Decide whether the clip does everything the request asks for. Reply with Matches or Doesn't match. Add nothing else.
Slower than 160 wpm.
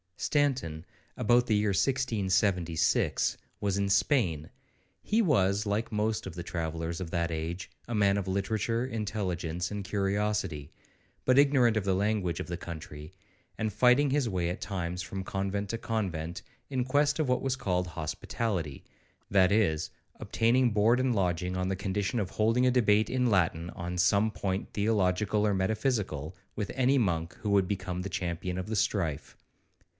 Doesn't match